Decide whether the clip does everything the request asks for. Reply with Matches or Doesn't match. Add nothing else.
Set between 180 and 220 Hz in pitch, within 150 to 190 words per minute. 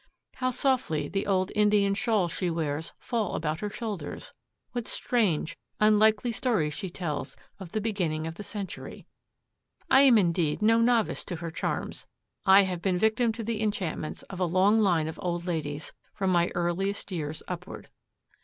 Matches